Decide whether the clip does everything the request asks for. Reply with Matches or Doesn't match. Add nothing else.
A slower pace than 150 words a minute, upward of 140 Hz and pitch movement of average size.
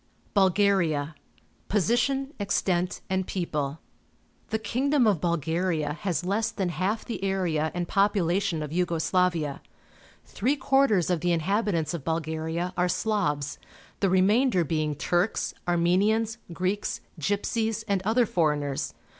Matches